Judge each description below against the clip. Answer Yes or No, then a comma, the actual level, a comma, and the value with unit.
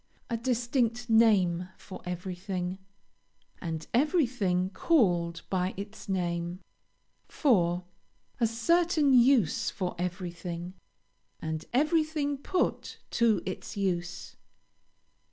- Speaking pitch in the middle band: No, high, 195 Hz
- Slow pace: Yes, slow, 90 wpm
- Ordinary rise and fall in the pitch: No, wide, 5.7 semitones